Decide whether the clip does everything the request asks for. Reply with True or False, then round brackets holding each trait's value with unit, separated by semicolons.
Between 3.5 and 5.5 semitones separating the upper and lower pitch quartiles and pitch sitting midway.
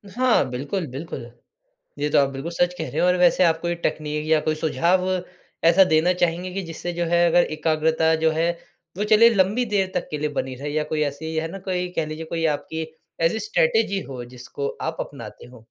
False (3.0 semitones; 165 Hz)